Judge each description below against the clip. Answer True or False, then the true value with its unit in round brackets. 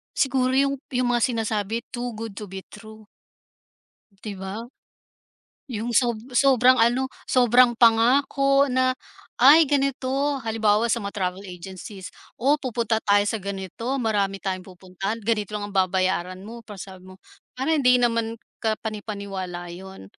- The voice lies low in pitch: False (225 Hz)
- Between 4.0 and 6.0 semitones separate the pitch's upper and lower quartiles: True (4.3 semitones)